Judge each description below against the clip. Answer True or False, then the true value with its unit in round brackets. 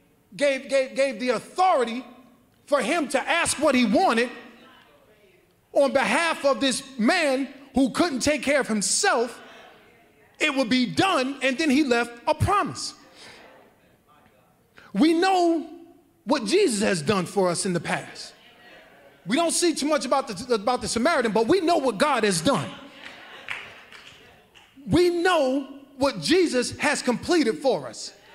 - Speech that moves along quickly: False (145 wpm)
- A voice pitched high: True (270 Hz)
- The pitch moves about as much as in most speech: True (4.3 semitones)